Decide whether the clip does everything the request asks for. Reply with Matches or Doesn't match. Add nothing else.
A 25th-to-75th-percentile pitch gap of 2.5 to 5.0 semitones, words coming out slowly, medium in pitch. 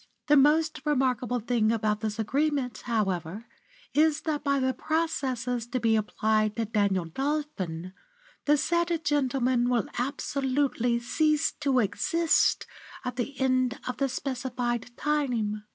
Doesn't match